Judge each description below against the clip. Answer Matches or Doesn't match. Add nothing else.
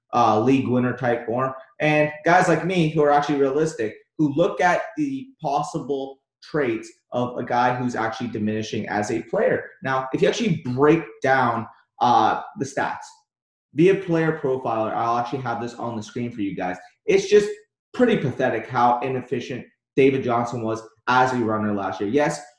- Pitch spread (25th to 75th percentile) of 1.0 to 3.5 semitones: Doesn't match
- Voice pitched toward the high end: Doesn't match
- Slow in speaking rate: Doesn't match